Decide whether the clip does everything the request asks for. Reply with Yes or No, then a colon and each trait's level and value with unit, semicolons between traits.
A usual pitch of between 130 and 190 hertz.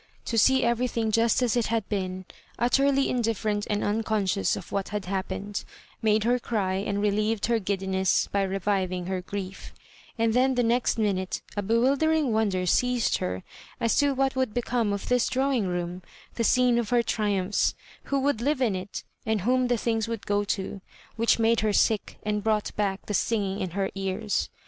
No: high, 215 Hz